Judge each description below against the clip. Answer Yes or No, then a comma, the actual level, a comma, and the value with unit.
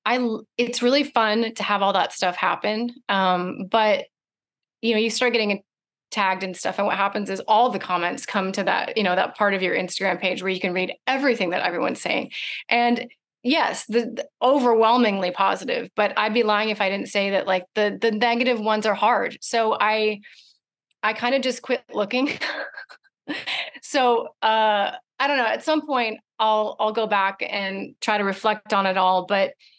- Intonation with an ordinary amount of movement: Yes, average, 3.8 semitones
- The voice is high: Yes, high, 215 Hz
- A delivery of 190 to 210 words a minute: Yes, average, 195 wpm